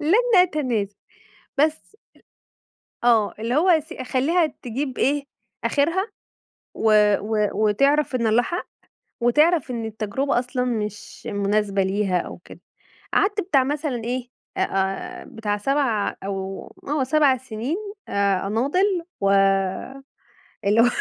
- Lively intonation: Yes, wide, 6.0 semitones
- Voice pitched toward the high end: Yes, very high, 250 Hz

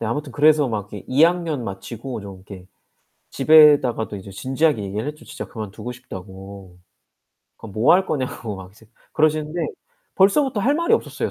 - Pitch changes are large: Yes, wide, 7.3 semitones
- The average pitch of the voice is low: Yes, low, 125 Hz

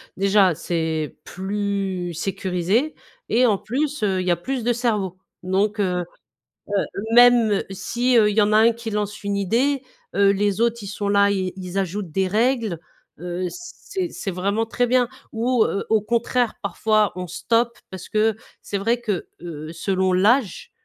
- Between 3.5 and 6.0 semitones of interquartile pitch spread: Yes, average, 3.8 semitones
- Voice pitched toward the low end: No, high, 205 Hz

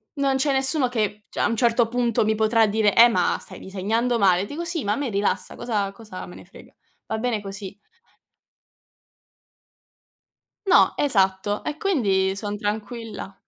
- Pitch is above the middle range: Yes, high, 220 Hz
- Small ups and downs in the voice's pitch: No, average, 3.6 semitones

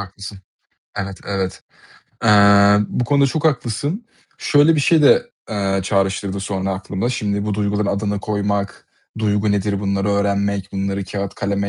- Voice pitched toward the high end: No, low, 100 Hz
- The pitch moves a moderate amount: No, narrow, 1.5 semitones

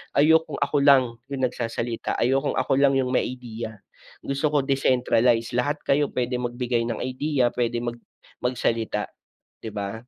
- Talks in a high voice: No, low, 125 Hz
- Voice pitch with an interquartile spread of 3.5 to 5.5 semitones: No, average, 2.7 semitones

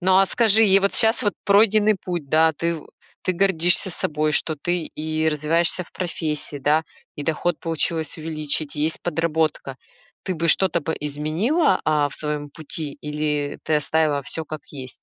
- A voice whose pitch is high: No, medium, 160 Hz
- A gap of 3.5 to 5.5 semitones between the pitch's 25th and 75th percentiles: No, average, 2.9 semitones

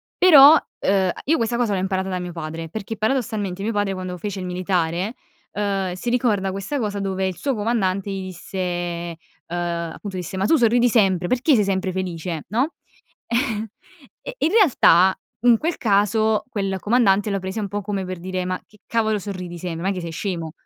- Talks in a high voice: Yes, high, 195 Hz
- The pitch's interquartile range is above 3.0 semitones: Yes, average, 3.4 semitones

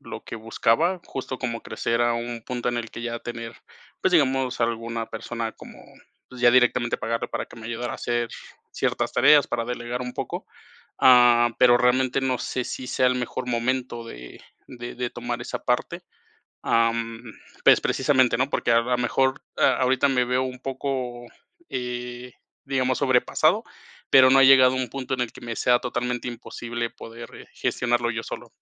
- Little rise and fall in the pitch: Yes, narrow, 1.5 semitones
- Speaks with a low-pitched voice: Yes, low, 125 Hz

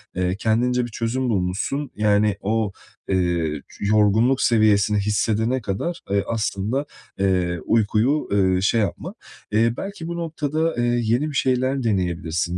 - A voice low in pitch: Yes, low, 110 Hz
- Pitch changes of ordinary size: Yes, average, 4.3 semitones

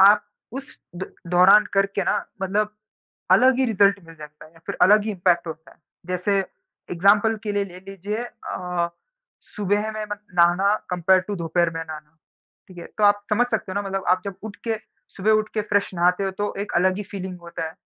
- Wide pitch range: No, average, 2.9 semitones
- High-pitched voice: Yes, high, 195 Hz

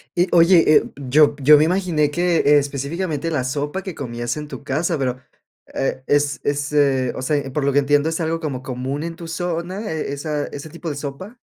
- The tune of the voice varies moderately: Yes, average, 3.0 semitones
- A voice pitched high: No, medium, 150 Hz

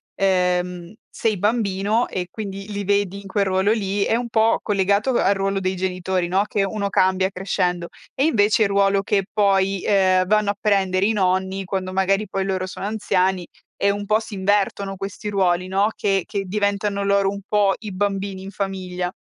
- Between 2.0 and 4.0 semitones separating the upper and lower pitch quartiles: No, narrow, 1.4 semitones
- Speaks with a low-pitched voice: No, high, 195 Hz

